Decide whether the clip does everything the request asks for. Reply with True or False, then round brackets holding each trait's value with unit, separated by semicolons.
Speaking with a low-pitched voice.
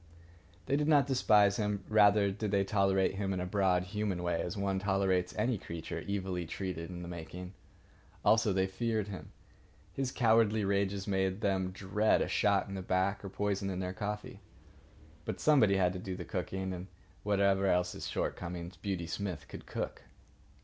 True (95 Hz)